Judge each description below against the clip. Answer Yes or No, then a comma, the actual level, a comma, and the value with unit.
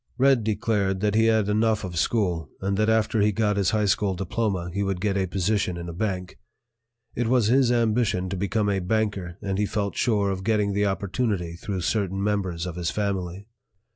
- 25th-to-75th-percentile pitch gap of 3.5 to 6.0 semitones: No, narrow, 2.6 semitones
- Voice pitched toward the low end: Yes, low, 100 Hz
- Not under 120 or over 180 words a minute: No, average, 200 wpm